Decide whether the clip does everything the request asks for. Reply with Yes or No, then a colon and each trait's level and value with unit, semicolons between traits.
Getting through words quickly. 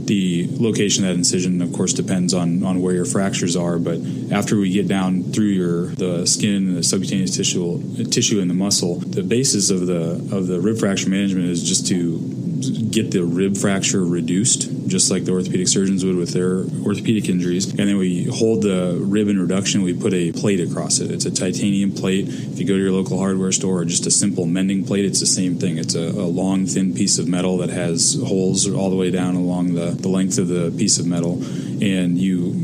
Yes: fast, 220 wpm